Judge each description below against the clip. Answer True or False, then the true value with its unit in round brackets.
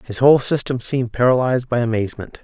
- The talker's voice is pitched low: True (125 Hz)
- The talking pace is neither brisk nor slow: True (175 wpm)